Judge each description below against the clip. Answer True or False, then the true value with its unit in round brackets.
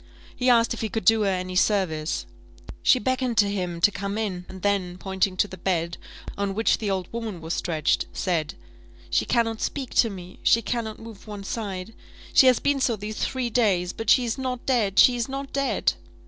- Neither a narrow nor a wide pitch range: True (4.1 semitones)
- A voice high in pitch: True (205 Hz)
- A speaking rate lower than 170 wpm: False (205 wpm)